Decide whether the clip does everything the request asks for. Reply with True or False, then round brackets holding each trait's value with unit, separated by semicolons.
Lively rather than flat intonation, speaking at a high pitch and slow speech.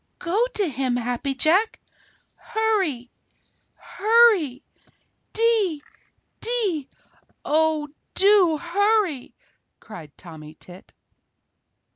True (8.5 semitones; 320 Hz; 80 wpm)